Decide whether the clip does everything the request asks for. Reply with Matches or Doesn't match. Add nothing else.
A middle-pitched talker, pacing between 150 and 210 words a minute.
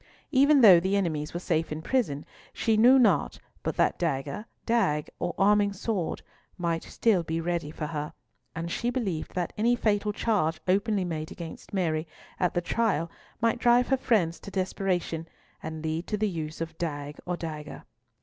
Matches